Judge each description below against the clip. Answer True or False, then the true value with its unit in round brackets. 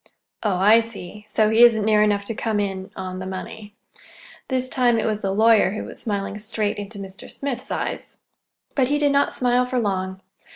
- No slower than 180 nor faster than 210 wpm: True (195 wpm)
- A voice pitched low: False (215 Hz)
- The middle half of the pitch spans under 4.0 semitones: True (2.9 semitones)